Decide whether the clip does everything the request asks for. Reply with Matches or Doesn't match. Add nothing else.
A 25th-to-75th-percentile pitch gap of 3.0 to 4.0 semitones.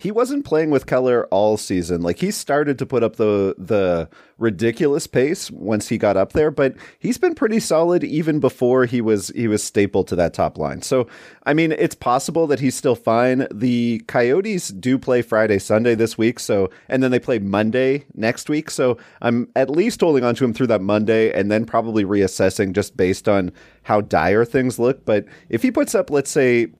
Doesn't match